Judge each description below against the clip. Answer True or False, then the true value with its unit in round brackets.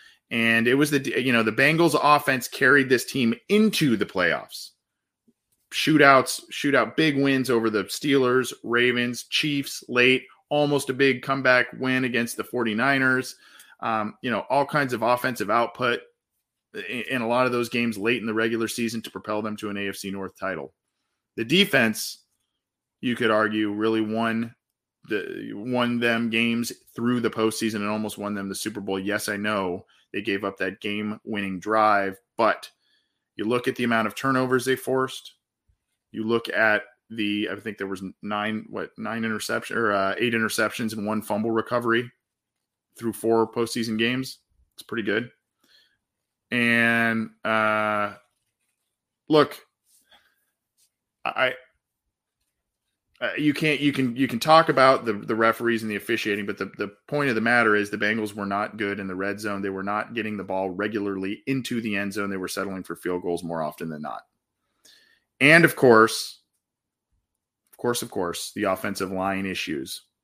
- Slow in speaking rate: False (165 wpm)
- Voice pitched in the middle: False (115 Hz)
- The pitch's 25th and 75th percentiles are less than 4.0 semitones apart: True (3.3 semitones)